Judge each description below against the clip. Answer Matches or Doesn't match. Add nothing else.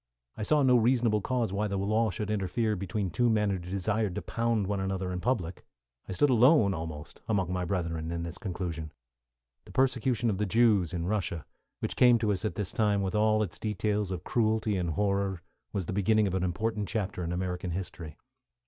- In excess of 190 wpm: Matches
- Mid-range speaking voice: Doesn't match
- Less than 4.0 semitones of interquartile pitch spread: Matches